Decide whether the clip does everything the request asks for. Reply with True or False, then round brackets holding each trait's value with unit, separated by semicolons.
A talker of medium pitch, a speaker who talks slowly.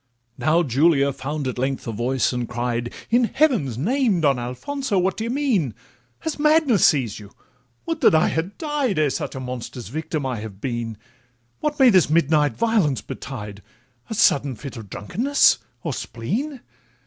False (150 Hz; 170 wpm)